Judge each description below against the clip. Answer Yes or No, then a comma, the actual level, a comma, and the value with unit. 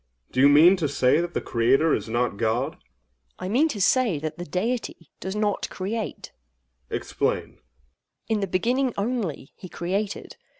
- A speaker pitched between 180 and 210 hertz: Yes, medium, 185 Hz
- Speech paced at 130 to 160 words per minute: No, average, 175 wpm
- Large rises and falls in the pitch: Yes, wide, 6.7 semitones